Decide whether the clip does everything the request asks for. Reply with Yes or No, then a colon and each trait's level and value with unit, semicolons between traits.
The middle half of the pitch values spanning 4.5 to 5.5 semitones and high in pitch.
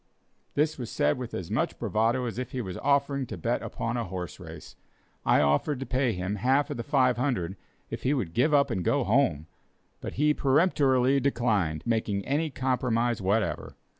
No: average, 5.2 semitones; low, 125 Hz